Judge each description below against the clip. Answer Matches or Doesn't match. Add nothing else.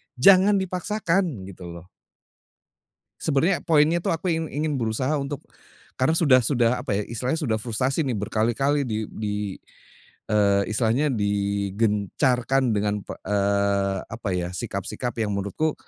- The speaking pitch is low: Matches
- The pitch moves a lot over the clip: Matches